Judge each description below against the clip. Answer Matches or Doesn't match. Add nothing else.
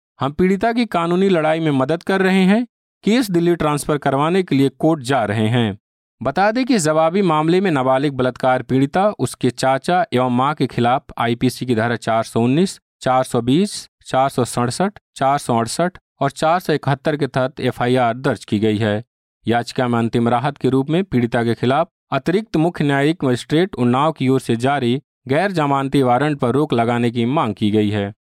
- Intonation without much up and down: Doesn't match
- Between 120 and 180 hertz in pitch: Matches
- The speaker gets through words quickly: Matches